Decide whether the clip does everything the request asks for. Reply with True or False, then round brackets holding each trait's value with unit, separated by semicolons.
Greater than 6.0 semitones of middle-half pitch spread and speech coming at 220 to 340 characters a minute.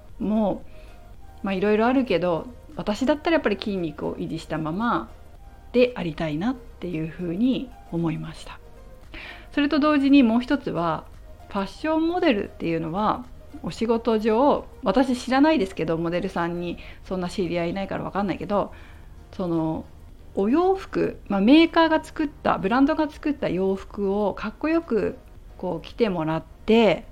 True (7.9 semitones; 330 characters per minute)